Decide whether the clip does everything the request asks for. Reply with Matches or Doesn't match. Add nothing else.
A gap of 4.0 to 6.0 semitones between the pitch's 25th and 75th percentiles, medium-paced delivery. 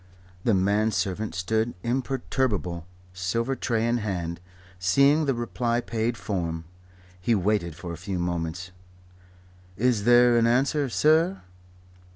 Doesn't match